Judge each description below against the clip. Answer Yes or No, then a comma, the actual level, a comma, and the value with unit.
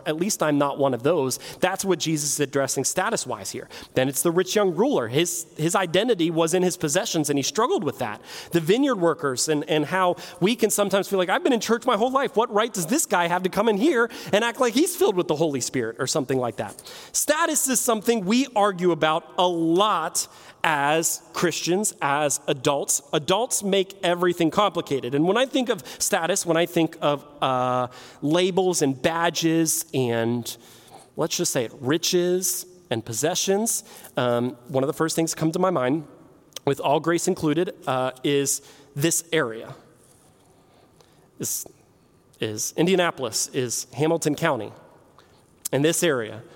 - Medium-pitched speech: Yes, medium, 165 Hz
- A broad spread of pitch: No, average, 4.7 semitones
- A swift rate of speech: No, average, 180 wpm